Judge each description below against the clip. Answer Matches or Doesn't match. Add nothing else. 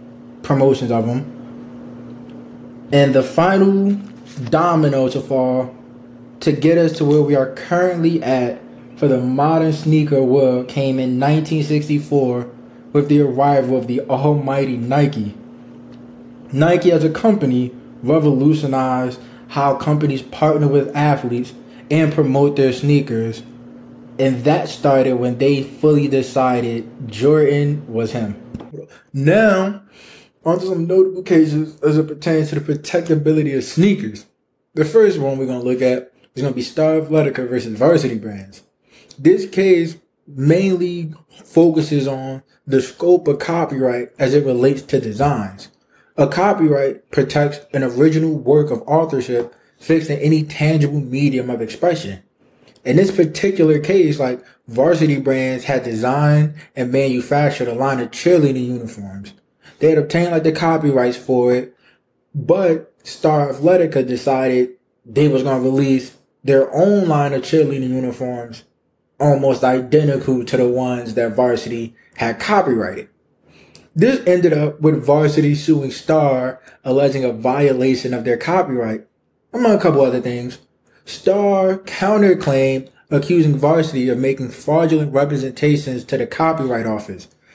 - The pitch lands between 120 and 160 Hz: Matches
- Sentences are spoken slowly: Matches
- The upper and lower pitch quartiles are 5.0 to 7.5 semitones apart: Doesn't match